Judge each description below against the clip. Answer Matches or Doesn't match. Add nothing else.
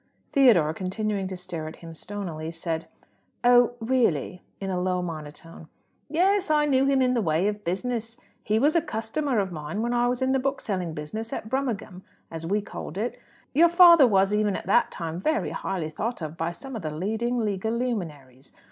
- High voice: Matches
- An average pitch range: Doesn't match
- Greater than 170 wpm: Matches